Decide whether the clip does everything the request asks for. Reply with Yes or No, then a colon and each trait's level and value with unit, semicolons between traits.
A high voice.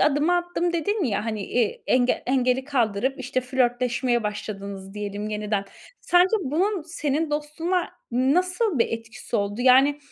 Yes: very high, 255 Hz